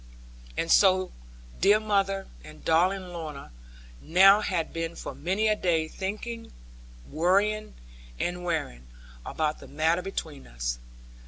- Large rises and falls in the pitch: No, average, 3.7 semitones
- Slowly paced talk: Yes, slow, 120 wpm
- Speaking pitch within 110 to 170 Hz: No, medium, 180 Hz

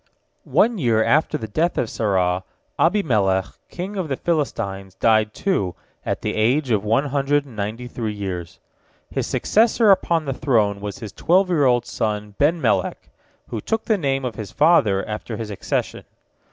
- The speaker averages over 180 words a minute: No, average, 165 wpm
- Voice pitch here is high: No, low, 120 Hz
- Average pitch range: No, wide, 7.0 semitones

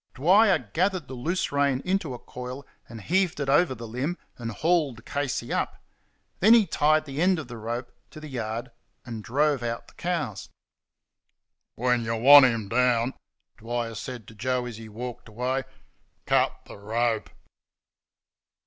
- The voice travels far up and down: No, average, 4.5 semitones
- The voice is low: Yes, low, 125 Hz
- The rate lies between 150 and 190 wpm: Yes, average, 160 wpm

